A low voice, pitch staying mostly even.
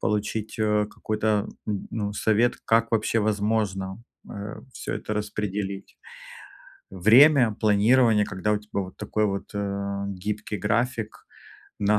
Yes: low, 105 Hz; narrow, 1.5 semitones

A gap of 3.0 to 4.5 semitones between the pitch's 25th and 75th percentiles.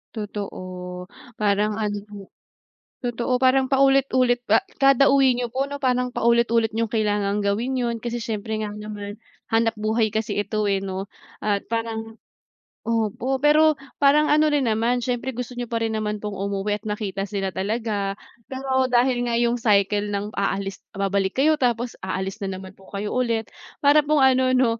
Yes: average, 3.5 semitones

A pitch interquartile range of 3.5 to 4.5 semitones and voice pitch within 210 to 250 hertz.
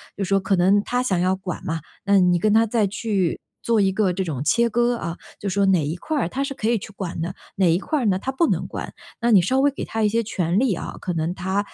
No: average, 4.1 semitones; high, 200 Hz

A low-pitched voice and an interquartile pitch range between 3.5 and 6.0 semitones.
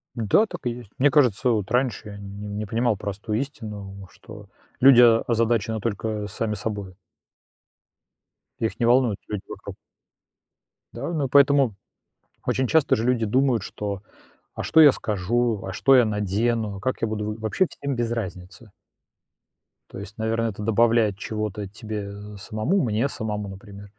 No: low, 110 Hz; average, 3.0 semitones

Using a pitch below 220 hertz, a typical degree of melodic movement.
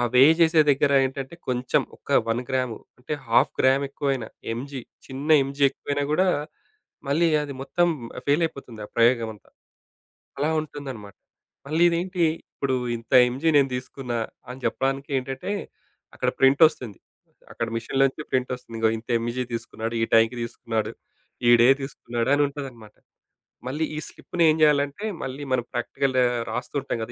Yes: low, 135 Hz; average, 3.2 semitones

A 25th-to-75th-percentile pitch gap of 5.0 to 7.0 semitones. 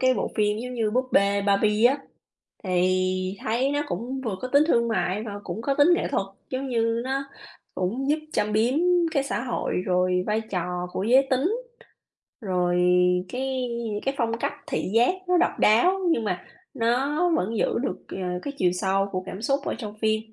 Yes: average, 5.3 semitones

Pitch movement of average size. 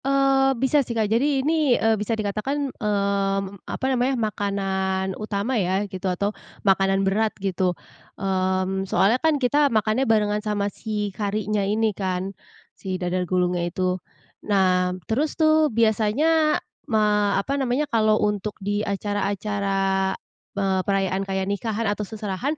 Yes: average, 3.2 semitones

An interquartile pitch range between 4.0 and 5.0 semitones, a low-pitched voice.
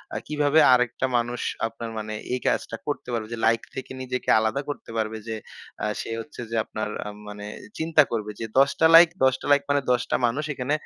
Yes: average, 4.3 semitones; low, 125 Hz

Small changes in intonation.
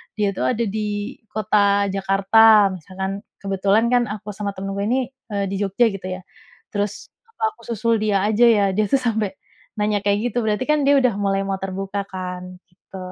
Yes: narrow, 2.1 semitones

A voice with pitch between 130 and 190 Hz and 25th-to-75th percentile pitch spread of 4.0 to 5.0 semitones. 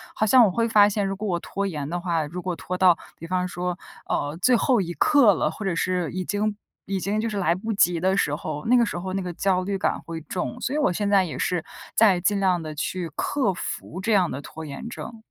No: medium, 185 Hz; average, 3.2 semitones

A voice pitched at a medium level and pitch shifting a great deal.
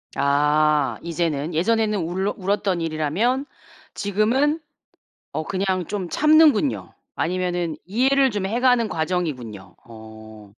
Yes: medium, 180 Hz; wide, 6.0 semitones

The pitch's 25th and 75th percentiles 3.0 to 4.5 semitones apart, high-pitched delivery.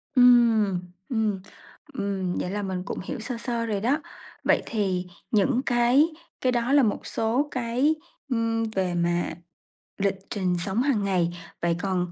Yes: average, 4.1 semitones; high, 220 Hz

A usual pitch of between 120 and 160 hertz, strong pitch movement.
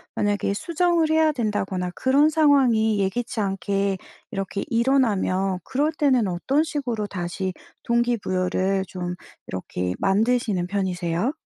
No: high, 205 Hz; wide, 5.8 semitones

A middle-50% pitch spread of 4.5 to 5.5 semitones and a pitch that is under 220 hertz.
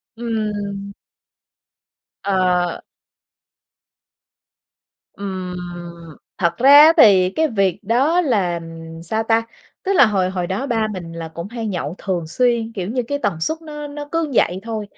Yes: average, 5.2 semitones; high, 210 Hz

